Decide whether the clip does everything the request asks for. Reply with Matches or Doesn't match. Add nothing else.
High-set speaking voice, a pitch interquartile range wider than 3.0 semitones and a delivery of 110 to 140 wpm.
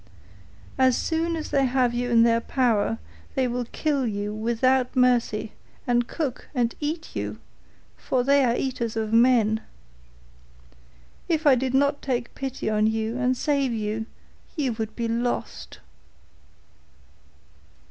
Doesn't match